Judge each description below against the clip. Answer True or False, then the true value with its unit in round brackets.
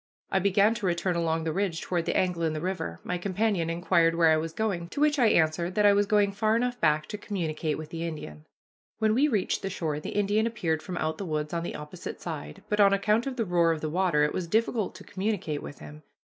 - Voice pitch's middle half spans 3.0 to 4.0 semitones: False (4.4 semitones)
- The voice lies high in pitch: False (180 Hz)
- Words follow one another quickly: True (250 wpm)